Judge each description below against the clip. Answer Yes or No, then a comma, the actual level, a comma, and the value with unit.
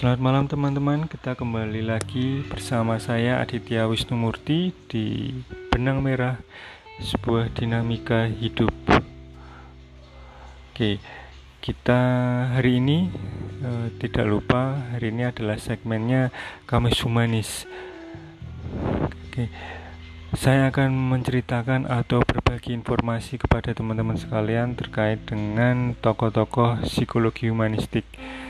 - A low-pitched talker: Yes, low, 115 Hz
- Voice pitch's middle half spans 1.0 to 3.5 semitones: Yes, narrow, 2.6 semitones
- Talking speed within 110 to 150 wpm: No, average, 95 wpm